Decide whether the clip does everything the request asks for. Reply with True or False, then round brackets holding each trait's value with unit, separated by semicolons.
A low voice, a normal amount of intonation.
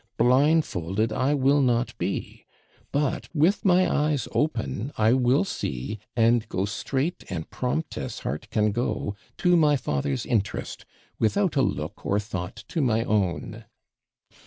False (120 Hz; 5.8 semitones)